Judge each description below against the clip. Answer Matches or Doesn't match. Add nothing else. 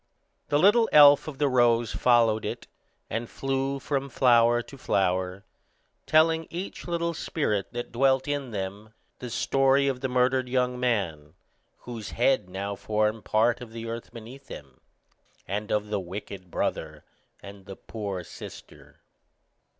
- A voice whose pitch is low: Matches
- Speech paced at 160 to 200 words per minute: Doesn't match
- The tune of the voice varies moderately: Matches